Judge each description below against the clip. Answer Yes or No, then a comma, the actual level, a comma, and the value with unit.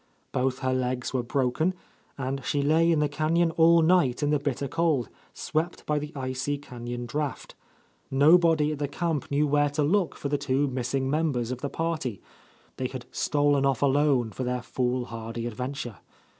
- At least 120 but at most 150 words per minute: No, average, 180 wpm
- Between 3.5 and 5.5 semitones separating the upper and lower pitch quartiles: No, average, 3.1 semitones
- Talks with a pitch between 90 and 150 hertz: Yes, medium, 140 Hz